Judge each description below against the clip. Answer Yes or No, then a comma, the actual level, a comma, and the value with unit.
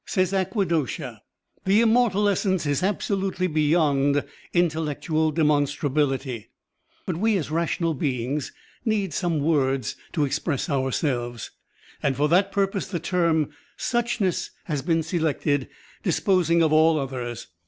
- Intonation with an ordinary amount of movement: Yes, average, 4.5 semitones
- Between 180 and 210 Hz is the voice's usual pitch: No, medium, 160 Hz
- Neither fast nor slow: No, slow, 120 wpm